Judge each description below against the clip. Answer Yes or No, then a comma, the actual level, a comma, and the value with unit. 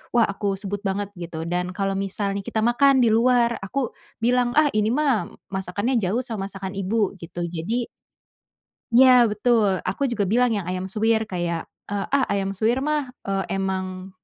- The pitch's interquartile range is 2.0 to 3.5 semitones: No, average, 3.9 semitones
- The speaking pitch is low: No, high, 205 Hz